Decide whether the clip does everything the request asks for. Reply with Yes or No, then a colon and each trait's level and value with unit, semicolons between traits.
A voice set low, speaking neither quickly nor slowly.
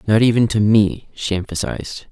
Yes: low, 105 Hz; average, 170 wpm